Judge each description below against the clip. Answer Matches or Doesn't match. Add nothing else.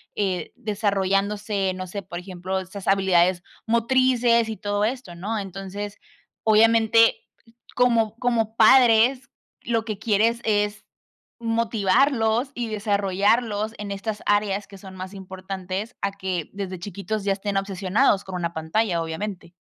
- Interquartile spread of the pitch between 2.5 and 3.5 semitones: Matches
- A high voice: Matches